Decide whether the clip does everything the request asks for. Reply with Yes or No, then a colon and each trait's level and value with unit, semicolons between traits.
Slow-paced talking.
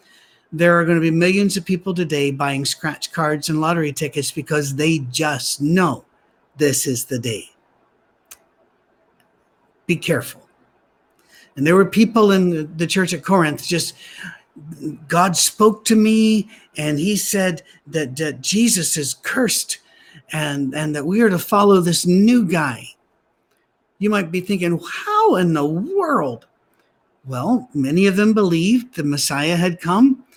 No: average, 145 wpm